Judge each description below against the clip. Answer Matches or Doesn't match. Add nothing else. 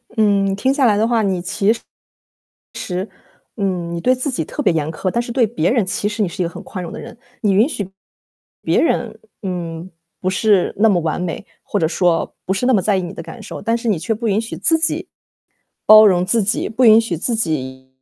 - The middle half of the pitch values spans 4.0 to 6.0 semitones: Matches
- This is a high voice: Matches